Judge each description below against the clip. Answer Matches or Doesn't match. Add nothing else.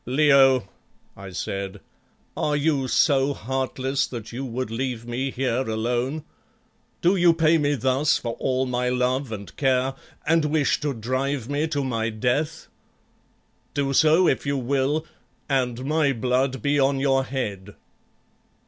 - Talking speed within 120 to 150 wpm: Matches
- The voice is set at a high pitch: Doesn't match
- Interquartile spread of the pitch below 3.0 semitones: Matches